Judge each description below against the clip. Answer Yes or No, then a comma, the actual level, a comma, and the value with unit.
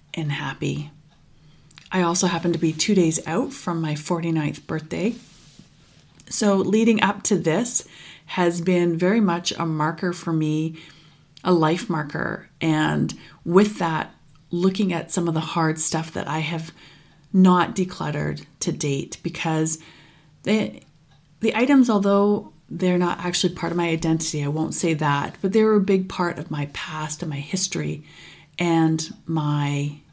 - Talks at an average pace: Yes, average, 155 wpm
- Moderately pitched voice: Yes, medium, 165 Hz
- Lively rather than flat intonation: No, average, 2.9 semitones